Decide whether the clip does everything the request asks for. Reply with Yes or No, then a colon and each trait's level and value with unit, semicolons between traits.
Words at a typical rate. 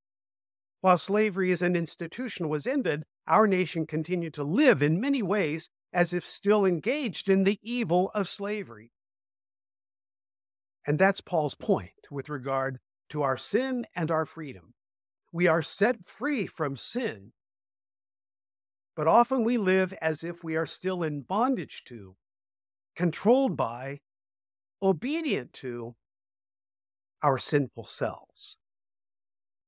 No: slow, 125 wpm